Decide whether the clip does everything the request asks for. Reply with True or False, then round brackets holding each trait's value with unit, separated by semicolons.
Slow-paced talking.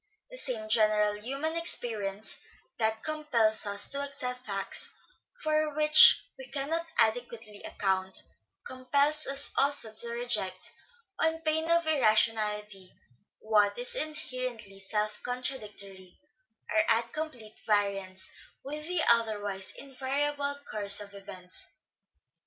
True (110 wpm)